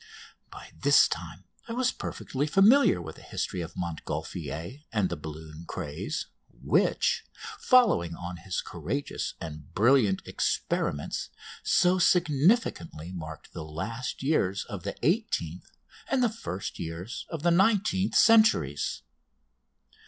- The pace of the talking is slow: Yes, slow, 125 wpm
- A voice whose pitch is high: No, low, 100 Hz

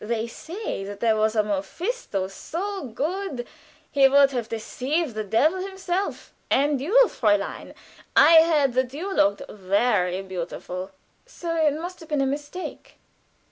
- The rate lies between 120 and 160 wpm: Yes, average, 140 wpm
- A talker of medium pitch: No, very high, 270 Hz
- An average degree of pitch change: No, wide, 7.7 semitones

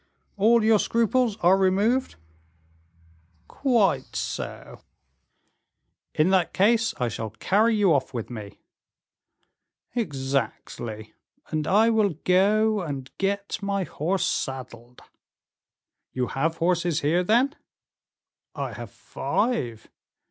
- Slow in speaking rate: Yes, slow, 105 wpm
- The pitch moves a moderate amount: No, wide, 8.2 semitones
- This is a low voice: No, medium, 185 Hz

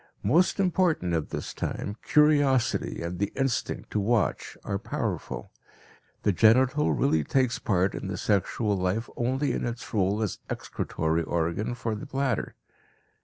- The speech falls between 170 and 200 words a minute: No, average, 145 wpm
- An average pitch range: No, wide, 5.7 semitones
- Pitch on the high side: No, low, 110 Hz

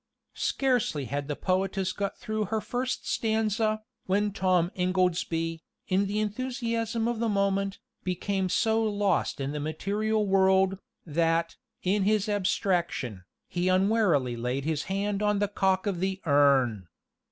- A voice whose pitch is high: Yes, high, 195 Hz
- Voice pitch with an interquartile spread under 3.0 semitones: No, average, 3.9 semitones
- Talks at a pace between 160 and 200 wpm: No, average, 140 wpm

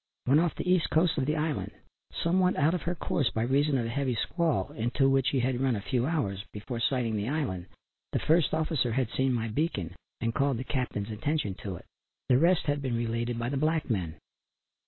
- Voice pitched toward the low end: Yes, low, 130 Hz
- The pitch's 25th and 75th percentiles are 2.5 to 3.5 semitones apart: No, average, 4.9 semitones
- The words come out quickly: Yes, fast, 220 wpm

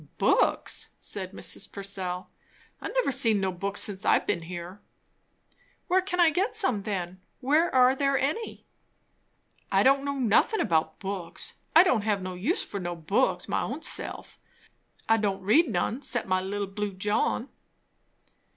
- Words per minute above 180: No, average, 160 wpm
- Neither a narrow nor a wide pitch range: No, wide, 6.5 semitones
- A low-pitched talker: No, high, 205 Hz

